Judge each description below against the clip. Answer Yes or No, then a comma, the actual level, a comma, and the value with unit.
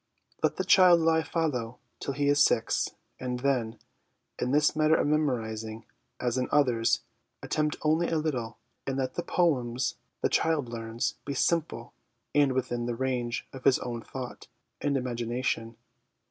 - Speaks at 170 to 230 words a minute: No, average, 160 wpm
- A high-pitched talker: No, low, 130 Hz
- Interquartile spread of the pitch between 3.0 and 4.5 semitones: Yes, average, 4.2 semitones